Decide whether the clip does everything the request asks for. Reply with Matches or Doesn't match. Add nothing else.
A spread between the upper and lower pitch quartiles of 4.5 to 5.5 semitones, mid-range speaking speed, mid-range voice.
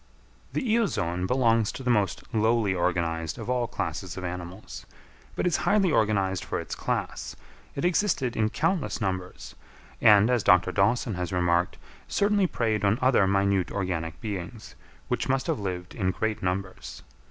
Doesn't match